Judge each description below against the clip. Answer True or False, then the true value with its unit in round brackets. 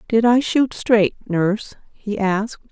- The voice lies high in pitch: True (215 Hz)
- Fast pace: False (155 wpm)